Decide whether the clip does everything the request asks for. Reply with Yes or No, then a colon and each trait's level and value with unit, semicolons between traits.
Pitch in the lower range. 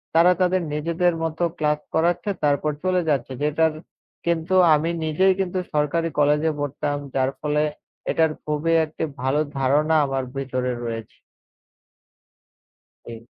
No: medium, 150 Hz